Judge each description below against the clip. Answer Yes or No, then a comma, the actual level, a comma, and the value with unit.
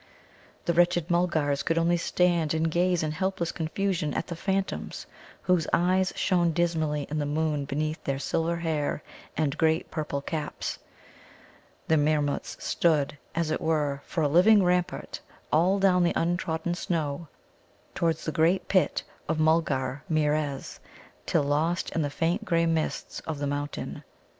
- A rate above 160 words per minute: No, average, 150 wpm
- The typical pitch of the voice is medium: Yes, medium, 160 Hz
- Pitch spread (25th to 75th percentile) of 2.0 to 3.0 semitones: Yes, narrow, 2.5 semitones